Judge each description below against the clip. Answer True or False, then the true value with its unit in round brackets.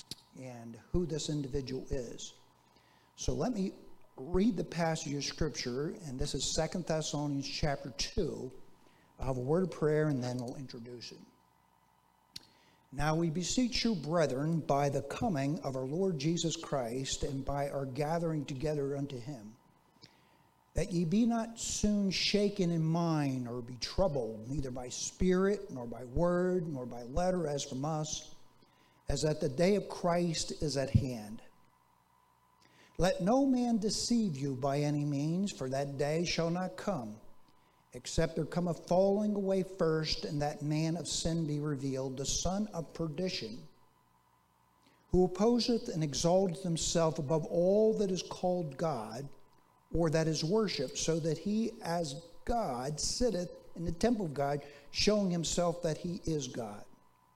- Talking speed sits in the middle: True (155 wpm)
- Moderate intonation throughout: True (4.7 semitones)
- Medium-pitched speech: True (155 Hz)